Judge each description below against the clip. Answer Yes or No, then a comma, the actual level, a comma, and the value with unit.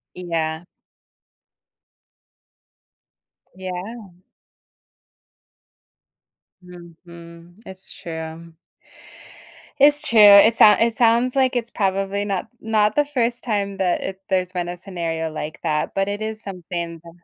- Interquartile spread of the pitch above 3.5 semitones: Yes, average, 4.3 semitones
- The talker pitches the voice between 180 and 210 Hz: Yes, high, 190 Hz